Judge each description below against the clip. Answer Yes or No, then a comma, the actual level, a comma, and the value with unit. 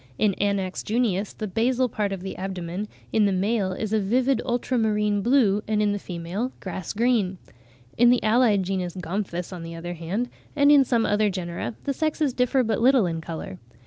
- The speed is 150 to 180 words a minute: No, average, 190 wpm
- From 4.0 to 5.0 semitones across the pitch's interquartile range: Yes, average, 4.4 semitones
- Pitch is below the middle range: No, high, 205 Hz